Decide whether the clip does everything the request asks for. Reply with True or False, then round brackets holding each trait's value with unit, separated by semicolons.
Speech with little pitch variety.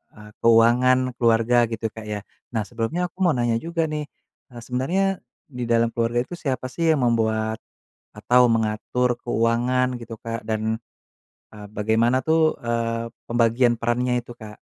True (1.8 semitones)